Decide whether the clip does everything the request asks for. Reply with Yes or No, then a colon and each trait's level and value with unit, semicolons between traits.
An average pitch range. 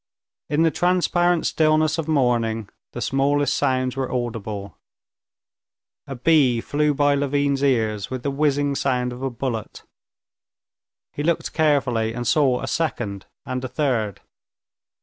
Yes: average, 3.4 semitones